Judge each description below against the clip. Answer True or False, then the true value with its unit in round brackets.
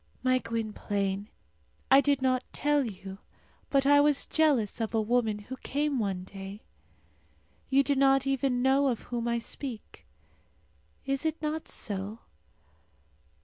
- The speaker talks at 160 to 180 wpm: False (140 wpm)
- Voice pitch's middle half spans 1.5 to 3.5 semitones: False (4.4 semitones)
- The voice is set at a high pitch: True (255 Hz)